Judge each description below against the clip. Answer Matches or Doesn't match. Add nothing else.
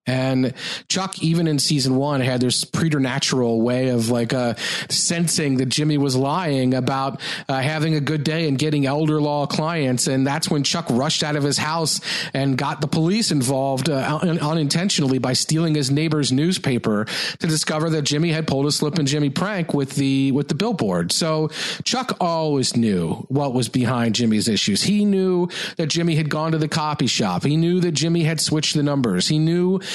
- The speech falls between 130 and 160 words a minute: Doesn't match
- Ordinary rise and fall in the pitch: Matches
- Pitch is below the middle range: Doesn't match